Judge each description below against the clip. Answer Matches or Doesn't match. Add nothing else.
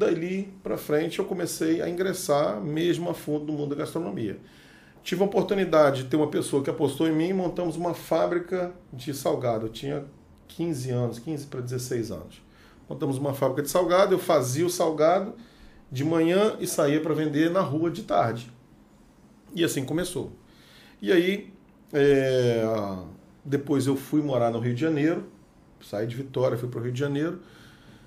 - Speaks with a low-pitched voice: Doesn't match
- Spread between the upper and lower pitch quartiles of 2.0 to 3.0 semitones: Doesn't match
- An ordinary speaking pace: Matches